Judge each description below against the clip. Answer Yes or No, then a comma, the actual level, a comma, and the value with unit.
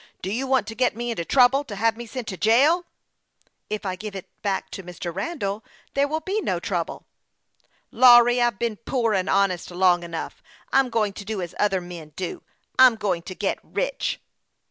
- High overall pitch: Yes, high, 220 Hz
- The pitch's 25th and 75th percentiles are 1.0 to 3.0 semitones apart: No, average, 4.7 semitones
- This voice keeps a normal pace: No, fast, 210 wpm